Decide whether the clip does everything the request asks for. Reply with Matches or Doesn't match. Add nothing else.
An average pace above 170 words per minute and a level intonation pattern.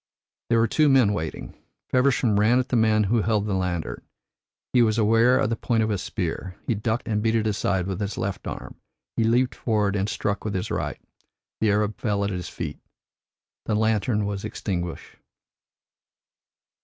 Matches